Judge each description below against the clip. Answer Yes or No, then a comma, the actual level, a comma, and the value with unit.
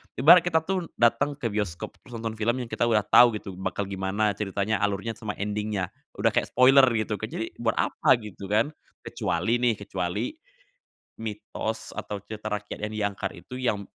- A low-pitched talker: Yes, low, 110 Hz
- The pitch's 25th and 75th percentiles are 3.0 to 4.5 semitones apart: No, narrow, 2.6 semitones